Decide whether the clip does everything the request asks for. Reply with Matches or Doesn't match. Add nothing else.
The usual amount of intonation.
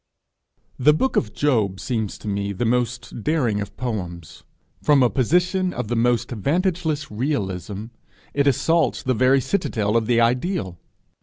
Doesn't match